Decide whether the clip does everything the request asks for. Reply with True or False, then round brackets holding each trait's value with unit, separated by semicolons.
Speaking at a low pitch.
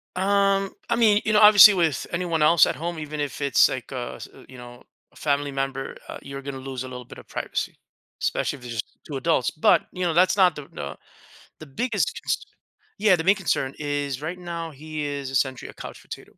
False (150 Hz)